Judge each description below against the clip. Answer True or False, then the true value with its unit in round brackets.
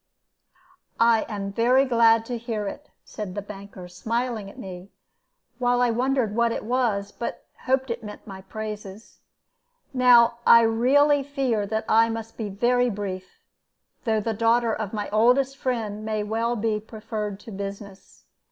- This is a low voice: False (225 Hz)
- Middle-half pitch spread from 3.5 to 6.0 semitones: False (2.7 semitones)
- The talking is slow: False (160 wpm)